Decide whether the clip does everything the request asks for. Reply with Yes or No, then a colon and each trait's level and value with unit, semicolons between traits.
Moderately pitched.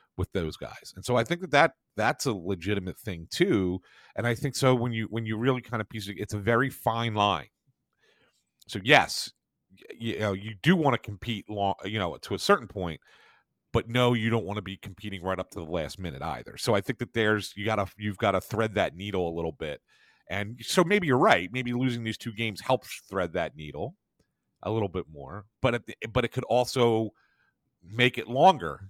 No: low, 110 Hz